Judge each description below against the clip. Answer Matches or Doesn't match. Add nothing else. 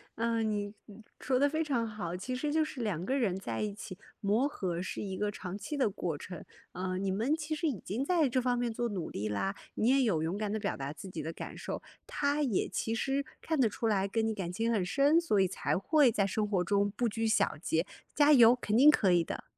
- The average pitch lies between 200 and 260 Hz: Matches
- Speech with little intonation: Doesn't match